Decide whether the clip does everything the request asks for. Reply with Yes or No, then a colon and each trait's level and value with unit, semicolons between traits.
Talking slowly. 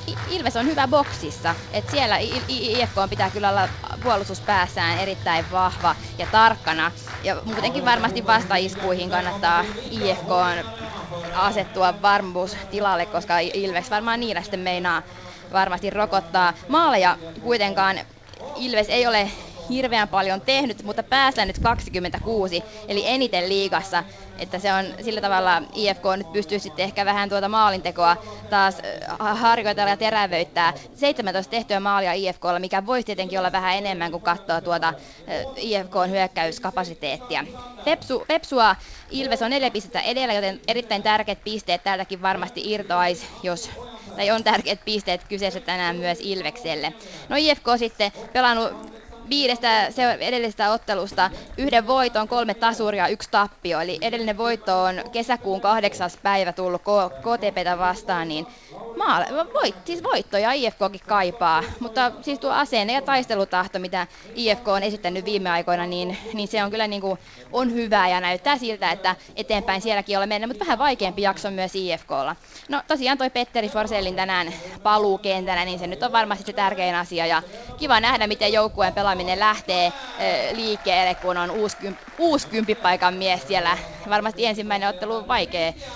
No: average, 145 wpm